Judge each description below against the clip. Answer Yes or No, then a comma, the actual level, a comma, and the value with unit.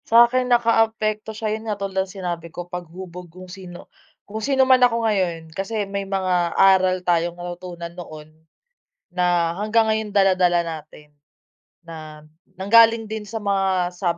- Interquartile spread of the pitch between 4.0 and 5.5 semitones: No, average, 3.6 semitones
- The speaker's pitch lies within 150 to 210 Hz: Yes, high, 190 Hz